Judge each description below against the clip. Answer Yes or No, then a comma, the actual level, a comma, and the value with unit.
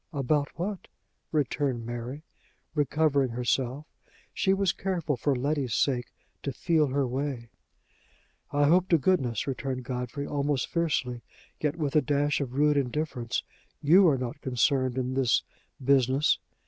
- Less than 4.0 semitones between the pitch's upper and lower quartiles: Yes, average, 3.1 semitones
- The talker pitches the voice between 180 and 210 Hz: No, medium, 140 Hz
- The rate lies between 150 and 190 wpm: No, slow, 135 wpm